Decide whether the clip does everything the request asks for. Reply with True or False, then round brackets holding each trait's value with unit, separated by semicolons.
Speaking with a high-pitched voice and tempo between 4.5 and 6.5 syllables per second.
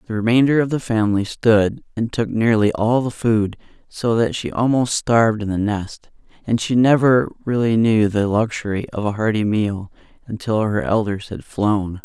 False (110 Hz; 4.7 syllables/s)